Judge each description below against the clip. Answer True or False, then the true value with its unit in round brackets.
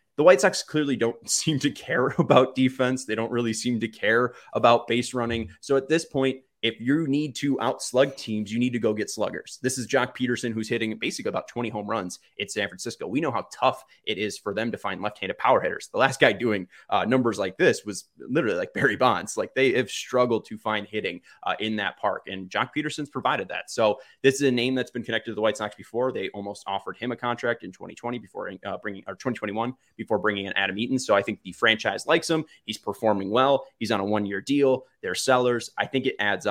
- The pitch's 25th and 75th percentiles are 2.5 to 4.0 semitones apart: True (3.4 semitones)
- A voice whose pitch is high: False (120 Hz)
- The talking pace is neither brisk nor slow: False (235 wpm)